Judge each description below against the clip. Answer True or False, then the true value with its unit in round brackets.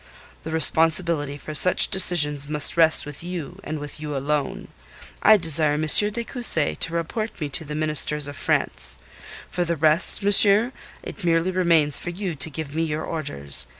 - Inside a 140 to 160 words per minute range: False (175 wpm)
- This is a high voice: False (160 Hz)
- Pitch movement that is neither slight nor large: True (3.0 semitones)